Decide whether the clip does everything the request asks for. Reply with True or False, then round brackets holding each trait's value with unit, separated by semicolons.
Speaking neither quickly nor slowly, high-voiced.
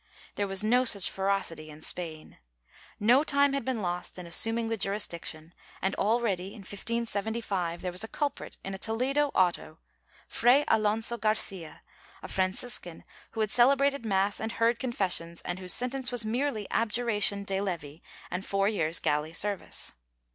True (165 wpm; 205 Hz)